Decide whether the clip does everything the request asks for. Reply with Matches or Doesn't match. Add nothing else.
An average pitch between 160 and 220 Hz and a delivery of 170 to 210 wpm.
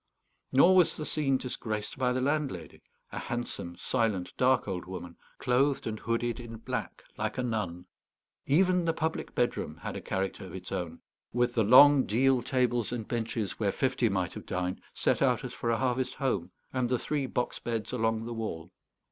Doesn't match